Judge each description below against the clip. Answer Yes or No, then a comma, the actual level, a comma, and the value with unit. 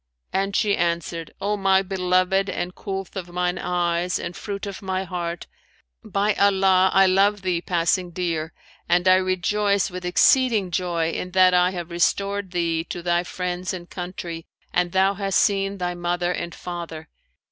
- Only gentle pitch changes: Yes, narrow, 1.8 semitones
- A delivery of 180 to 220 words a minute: No, average, 165 wpm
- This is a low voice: No, medium, 180 Hz